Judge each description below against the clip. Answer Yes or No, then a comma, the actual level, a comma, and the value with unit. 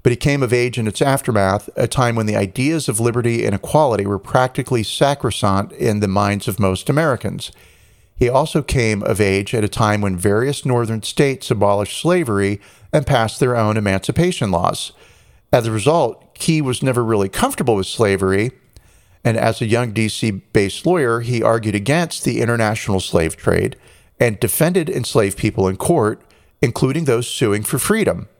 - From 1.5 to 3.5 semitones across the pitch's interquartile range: No, average, 4.0 semitones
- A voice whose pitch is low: Yes, low, 110 Hz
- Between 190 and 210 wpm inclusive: No, average, 170 wpm